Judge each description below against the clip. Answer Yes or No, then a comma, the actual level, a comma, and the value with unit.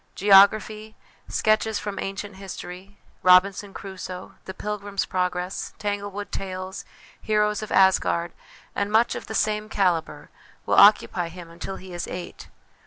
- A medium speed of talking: No, slow, 130 wpm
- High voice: Yes, high, 195 Hz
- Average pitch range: No, narrow, 2.3 semitones